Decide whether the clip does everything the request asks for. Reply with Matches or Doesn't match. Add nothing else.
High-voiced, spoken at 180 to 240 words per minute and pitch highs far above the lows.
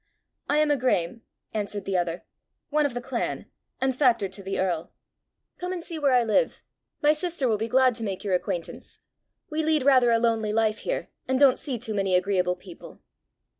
Matches